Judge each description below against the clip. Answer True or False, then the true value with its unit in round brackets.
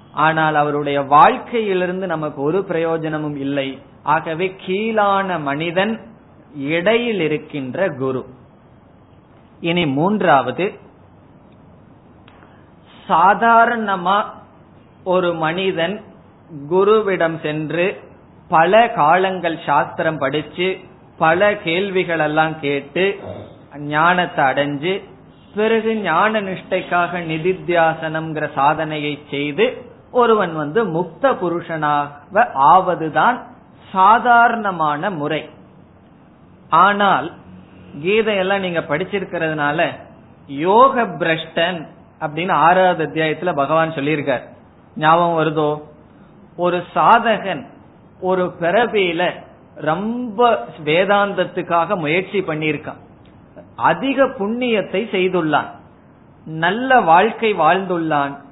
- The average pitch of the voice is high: False (170 Hz)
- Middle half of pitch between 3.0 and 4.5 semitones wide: True (4.2 semitones)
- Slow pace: True (65 wpm)